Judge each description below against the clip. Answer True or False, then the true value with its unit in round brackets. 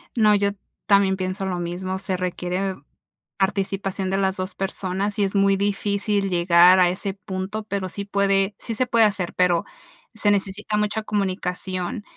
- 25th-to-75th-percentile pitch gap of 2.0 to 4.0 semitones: False (1.5 semitones)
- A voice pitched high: True (195 Hz)